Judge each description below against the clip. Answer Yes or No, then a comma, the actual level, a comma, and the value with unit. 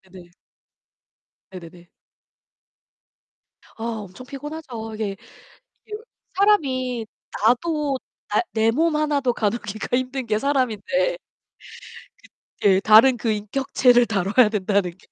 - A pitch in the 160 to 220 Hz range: No, high, 235 Hz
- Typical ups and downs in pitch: Yes, average, 4.6 semitones